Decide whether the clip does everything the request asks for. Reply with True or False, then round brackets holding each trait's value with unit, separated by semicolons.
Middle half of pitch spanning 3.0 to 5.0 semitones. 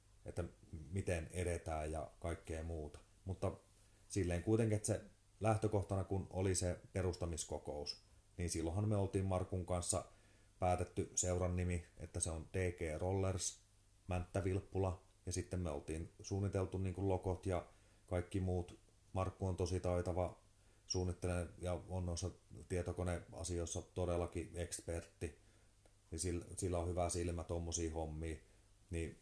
False (2.4 semitones)